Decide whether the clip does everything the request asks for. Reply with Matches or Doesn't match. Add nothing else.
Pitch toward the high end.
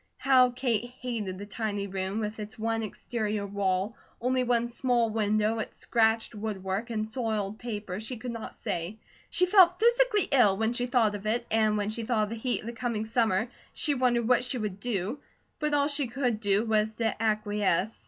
Matches